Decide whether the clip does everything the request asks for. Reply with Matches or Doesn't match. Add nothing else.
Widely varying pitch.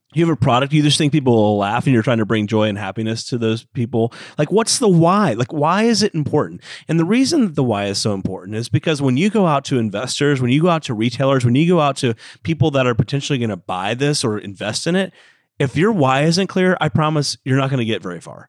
Matches